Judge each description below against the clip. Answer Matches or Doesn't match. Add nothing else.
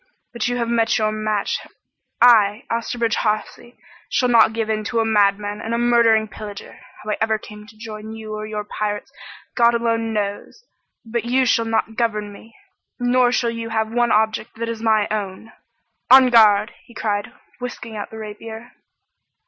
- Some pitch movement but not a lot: Doesn't match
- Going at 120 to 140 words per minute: Doesn't match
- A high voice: Matches